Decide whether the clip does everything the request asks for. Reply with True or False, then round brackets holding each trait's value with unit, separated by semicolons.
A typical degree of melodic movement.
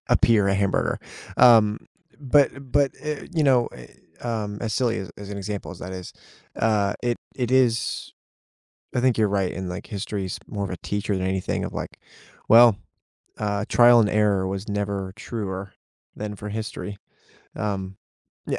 True (3.0 semitones)